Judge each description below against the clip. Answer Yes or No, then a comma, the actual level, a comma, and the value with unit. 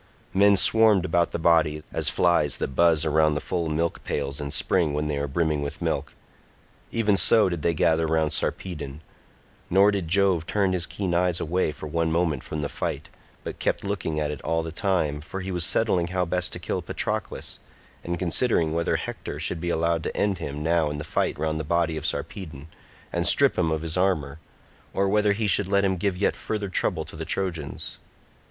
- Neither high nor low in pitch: No, very low, 85 Hz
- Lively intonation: No, average, 3.2 semitones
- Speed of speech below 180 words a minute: No, fast, 205 wpm